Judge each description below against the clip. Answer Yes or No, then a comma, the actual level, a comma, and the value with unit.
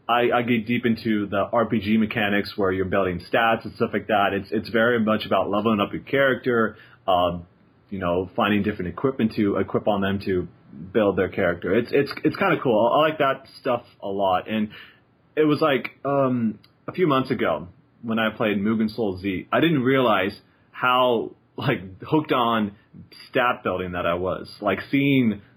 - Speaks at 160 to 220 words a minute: Yes, average, 190 wpm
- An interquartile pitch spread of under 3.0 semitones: No, average, 3.5 semitones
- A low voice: Yes, low, 110 Hz